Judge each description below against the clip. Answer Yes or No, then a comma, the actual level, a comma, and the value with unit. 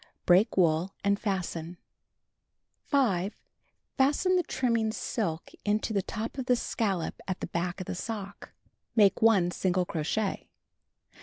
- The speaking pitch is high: Yes, high, 200 Hz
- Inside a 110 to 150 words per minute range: Yes, slow, 135 wpm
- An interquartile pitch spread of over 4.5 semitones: No, average, 4.1 semitones